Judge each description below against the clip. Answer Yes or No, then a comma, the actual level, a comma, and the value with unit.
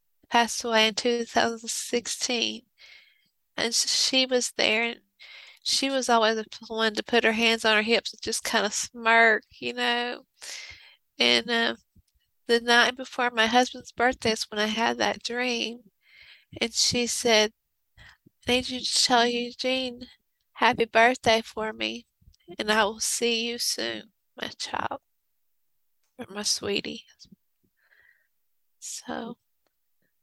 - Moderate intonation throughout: No, narrow, 2.0 semitones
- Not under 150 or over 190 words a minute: No, slow, 135 wpm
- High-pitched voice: Yes, high, 230 Hz